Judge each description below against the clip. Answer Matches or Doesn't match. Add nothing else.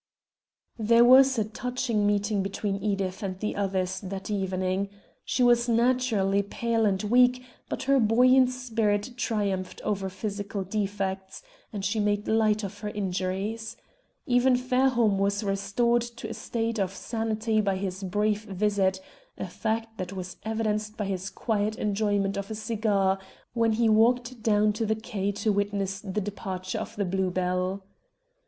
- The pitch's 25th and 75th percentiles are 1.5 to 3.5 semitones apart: Matches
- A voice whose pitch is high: Matches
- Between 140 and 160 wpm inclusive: Matches